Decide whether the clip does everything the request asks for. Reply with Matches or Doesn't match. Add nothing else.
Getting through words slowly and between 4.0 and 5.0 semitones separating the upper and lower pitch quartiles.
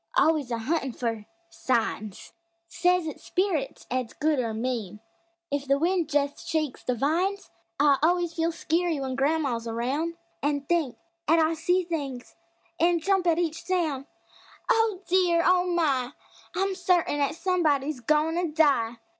Doesn't match